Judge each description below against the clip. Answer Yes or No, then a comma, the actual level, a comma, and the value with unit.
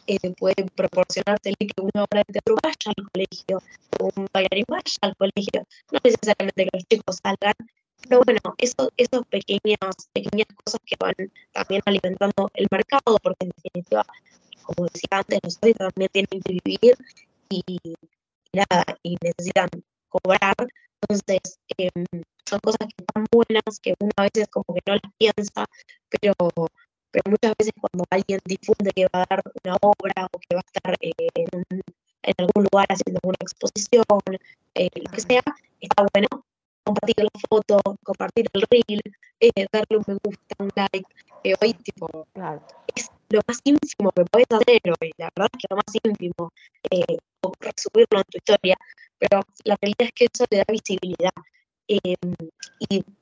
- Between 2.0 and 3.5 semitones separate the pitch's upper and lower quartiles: Yes, average, 2.8 semitones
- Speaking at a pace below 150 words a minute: No, average, 160 wpm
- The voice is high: Yes, high, 200 Hz